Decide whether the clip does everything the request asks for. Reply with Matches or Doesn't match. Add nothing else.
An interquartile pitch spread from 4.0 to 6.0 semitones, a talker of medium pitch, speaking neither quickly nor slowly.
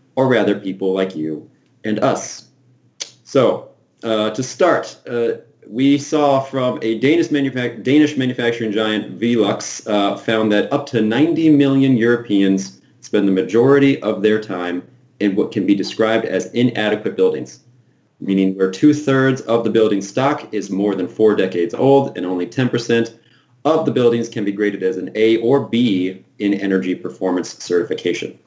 Doesn't match